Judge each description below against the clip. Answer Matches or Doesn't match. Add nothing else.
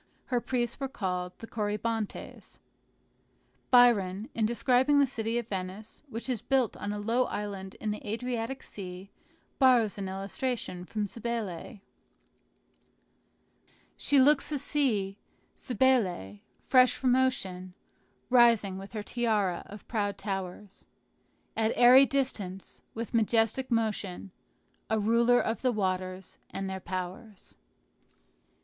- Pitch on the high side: Matches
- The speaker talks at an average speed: Doesn't match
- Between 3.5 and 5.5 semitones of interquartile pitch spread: Matches